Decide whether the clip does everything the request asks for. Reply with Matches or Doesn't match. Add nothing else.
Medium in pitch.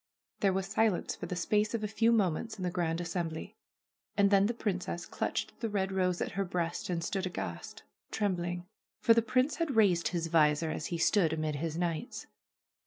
Matches